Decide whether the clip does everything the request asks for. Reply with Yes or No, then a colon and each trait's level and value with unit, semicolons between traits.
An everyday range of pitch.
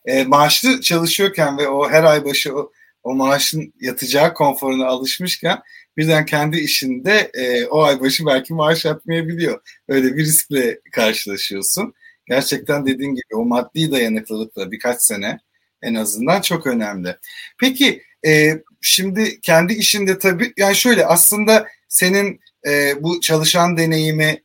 No: wide, 6.0 semitones